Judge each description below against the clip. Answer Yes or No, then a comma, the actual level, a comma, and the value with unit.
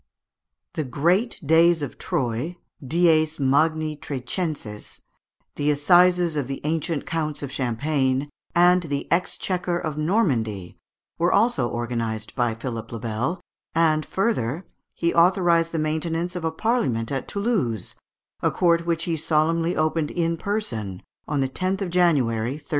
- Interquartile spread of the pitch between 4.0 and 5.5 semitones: Yes, average, 4.7 semitones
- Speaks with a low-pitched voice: No, medium, 155 Hz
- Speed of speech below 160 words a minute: Yes, average, 140 wpm